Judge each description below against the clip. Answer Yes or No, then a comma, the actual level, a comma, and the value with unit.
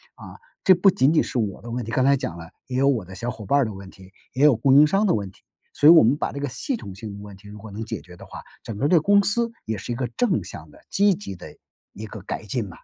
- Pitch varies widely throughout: Yes, wide, 6.7 semitones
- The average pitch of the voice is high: No, low, 120 Hz